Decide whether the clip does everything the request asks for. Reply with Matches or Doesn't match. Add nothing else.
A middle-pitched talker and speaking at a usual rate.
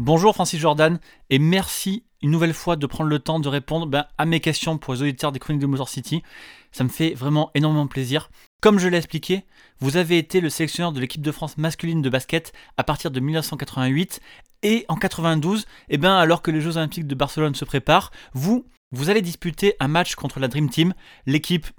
Matches